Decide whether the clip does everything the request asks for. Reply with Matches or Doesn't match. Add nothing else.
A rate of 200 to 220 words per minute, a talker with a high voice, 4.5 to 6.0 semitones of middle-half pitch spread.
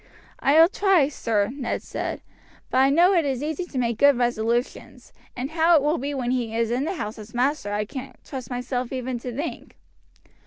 Doesn't match